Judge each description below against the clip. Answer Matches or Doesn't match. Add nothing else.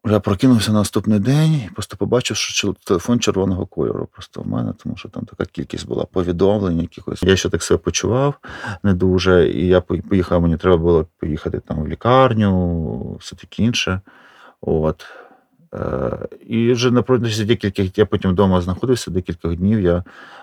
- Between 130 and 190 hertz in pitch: Doesn't match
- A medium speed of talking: Doesn't match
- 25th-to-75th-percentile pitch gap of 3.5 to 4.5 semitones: Matches